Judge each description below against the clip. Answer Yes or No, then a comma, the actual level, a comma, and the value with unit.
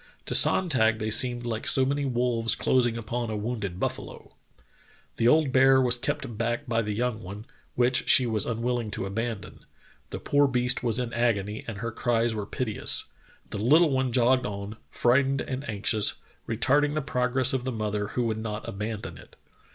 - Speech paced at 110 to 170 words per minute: No, average, 180 wpm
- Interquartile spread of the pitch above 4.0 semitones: No, average, 2.9 semitones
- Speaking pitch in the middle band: No, low, 120 Hz